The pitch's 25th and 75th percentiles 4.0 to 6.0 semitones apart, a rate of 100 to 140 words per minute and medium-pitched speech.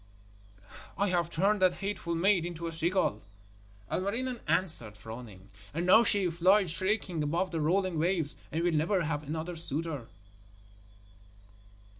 No: average, 3.1 semitones; slow, 135 wpm; medium, 170 Hz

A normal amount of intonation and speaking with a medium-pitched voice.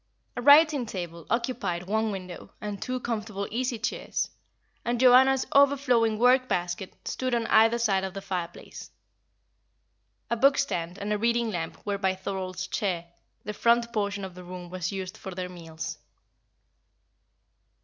No: average, 4.4 semitones; high, 205 Hz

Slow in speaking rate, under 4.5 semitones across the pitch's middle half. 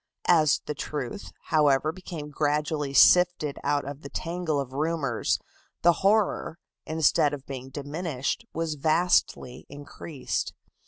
Yes: slow, 120 wpm; average, 2.8 semitones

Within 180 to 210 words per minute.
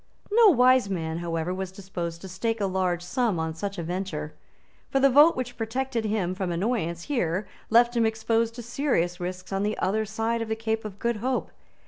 Yes: average, 200 wpm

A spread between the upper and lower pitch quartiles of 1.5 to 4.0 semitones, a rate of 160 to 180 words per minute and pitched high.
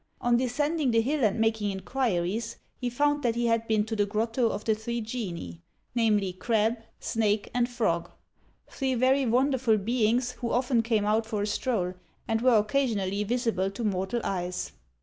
Yes: average, 2.9 semitones; average, 170 wpm; high, 225 Hz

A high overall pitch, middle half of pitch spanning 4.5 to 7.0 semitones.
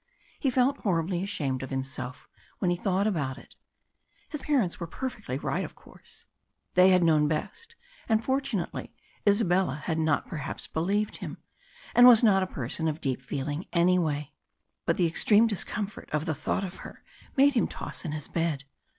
No: medium, 175 Hz; wide, 5.6 semitones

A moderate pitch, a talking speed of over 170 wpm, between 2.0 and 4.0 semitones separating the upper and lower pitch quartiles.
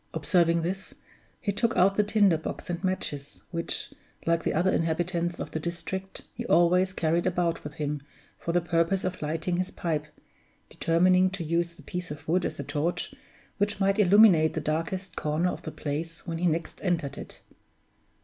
Yes: medium, 170 Hz; average, 180 wpm; narrow, 2.5 semitones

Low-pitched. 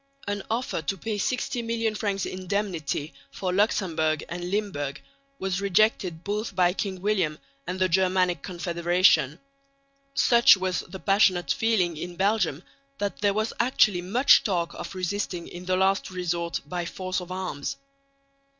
No: medium, 185 Hz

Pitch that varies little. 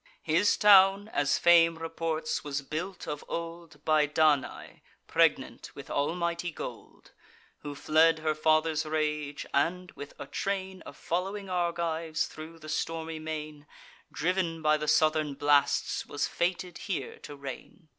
Yes: narrow, 2.1 semitones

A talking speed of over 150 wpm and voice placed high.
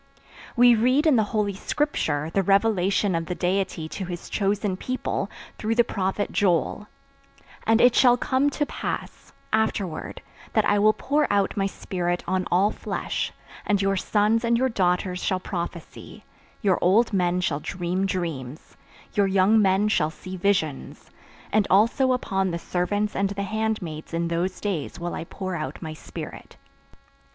Yes: average, 160 wpm; high, 195 Hz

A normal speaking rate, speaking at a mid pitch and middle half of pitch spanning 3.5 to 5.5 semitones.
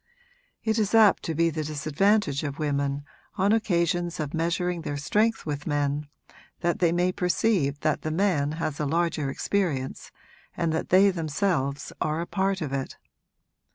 Yes: average, 160 wpm; medium, 165 Hz; average, 4.2 semitones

